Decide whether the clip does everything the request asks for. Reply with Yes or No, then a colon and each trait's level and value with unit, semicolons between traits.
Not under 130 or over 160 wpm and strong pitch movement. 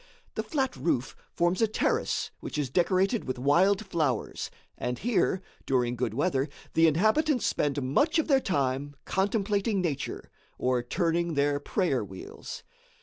Yes: average, 145 wpm; wide, 6.8 semitones